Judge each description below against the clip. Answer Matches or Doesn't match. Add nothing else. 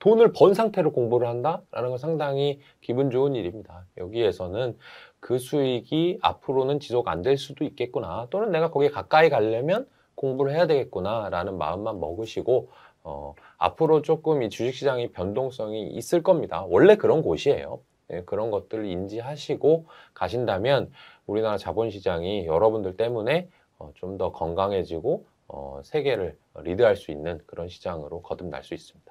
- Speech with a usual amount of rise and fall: Doesn't match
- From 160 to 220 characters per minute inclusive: Doesn't match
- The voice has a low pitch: Matches